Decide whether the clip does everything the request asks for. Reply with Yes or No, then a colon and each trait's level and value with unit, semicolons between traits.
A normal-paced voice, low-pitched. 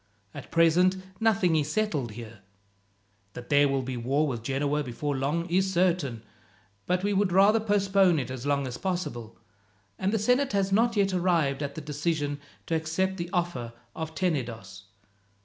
No: average, 165 wpm; medium, 160 Hz